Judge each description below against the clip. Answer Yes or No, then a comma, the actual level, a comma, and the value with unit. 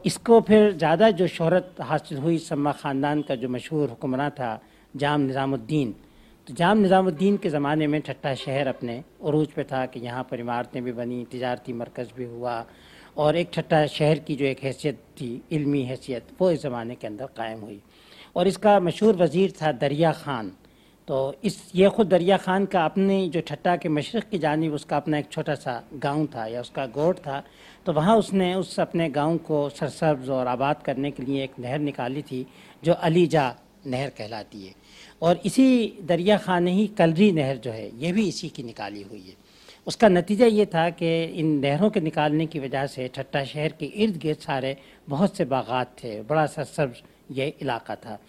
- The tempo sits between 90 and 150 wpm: No, fast, 190 wpm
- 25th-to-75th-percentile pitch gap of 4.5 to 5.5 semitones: Yes, average, 4.9 semitones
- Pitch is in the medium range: Yes, medium, 150 Hz